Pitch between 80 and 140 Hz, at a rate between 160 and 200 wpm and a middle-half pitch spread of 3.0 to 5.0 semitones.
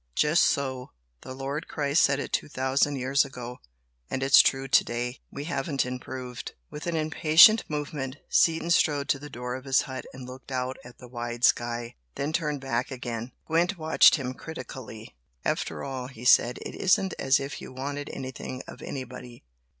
No: low, 135 Hz; average, 180 wpm; narrow, 2.5 semitones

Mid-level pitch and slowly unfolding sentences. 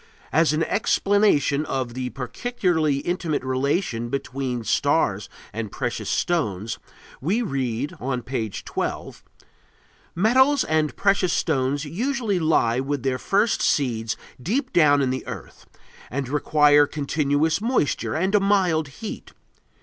Yes: medium, 145 Hz; slow, 125 wpm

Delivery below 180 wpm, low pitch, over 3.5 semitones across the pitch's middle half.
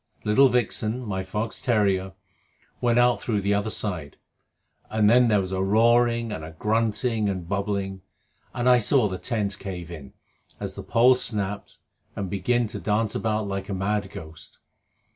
No: average, 165 wpm; low, 105 Hz; average, 3.2 semitones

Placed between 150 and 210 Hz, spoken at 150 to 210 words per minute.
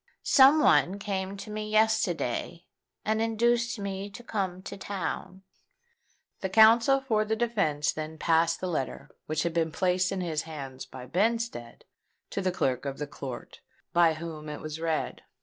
Yes: medium, 185 Hz; average, 165 wpm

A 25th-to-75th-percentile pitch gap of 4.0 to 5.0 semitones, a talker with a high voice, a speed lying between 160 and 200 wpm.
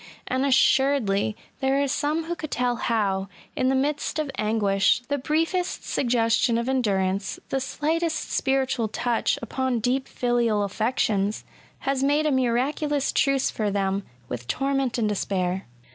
No: average, 4.5 semitones; very high, 250 Hz; average, 145 wpm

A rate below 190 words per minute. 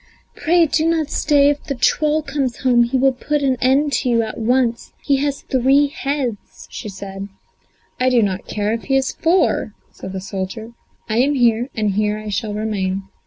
No: average, 195 wpm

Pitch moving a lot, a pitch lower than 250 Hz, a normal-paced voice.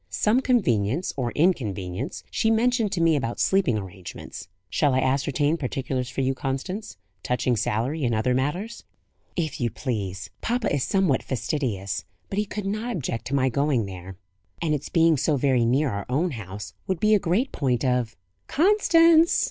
Yes: wide, 8.0 semitones; low, 135 Hz; average, 170 wpm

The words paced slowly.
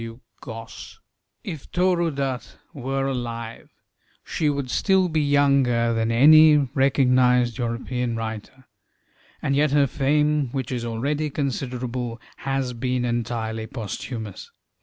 Yes: slow, 110 wpm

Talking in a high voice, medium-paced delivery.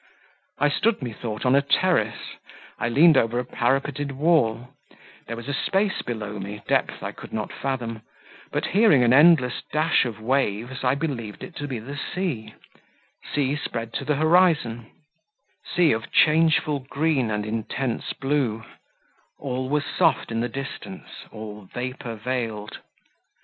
No: low, 130 Hz; average, 145 wpm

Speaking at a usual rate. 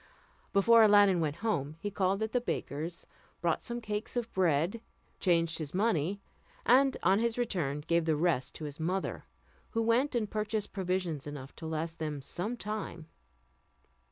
Yes: average, 160 wpm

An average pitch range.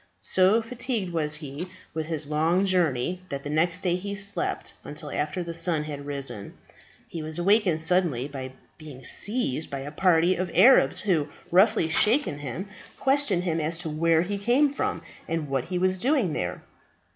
Yes: average, 4.0 semitones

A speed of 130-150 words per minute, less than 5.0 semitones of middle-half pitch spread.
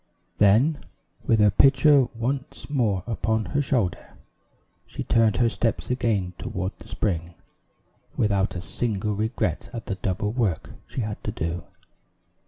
Yes: average, 140 wpm; average, 3.7 semitones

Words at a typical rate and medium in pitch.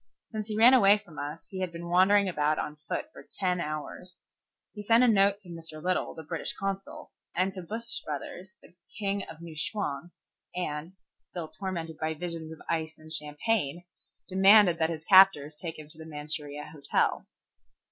Yes: average, 180 wpm; medium, 170 Hz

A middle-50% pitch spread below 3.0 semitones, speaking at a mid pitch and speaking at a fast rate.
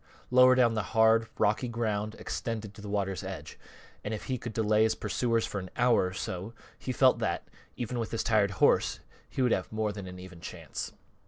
No: narrow, 2.4 semitones; low, 110 Hz; fast, 210 wpm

